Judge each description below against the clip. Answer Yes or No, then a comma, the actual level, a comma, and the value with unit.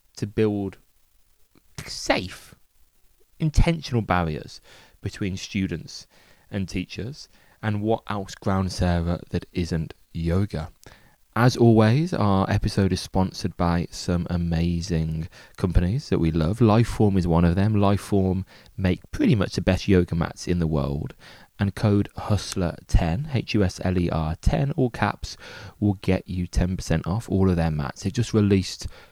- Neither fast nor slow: Yes, average, 145 wpm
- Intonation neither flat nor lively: Yes, average, 3.2 semitones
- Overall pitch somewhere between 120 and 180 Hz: No, very low, 95 Hz